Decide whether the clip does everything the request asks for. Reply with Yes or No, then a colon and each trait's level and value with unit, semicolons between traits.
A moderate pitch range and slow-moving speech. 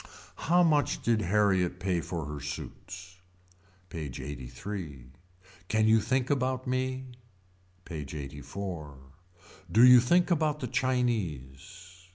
No: wide, 7.8 semitones; slow, 115 wpm